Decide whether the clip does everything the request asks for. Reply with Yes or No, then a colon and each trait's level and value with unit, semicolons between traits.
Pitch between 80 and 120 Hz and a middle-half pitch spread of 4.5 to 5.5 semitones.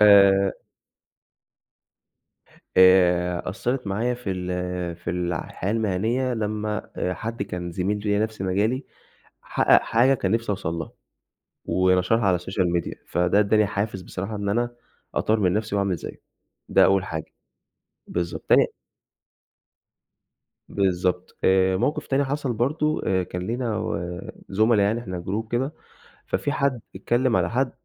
No: low, 100 Hz; average, 3.9 semitones